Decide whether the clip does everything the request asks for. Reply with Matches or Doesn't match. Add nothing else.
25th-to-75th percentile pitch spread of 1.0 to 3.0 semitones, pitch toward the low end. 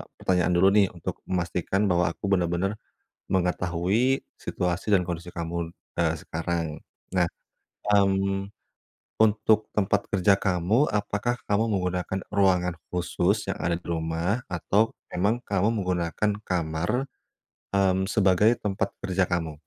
Matches